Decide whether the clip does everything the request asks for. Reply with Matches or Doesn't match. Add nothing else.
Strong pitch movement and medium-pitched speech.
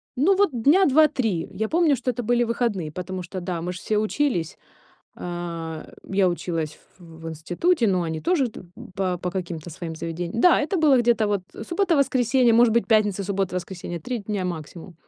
Doesn't match